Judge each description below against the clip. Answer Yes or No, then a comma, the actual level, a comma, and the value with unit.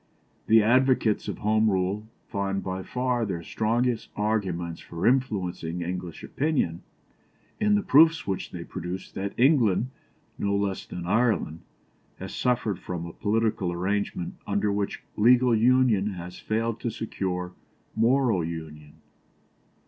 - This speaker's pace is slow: Yes, slow, 130 wpm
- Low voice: Yes, low, 105 Hz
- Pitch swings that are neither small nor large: Yes, average, 4.7 semitones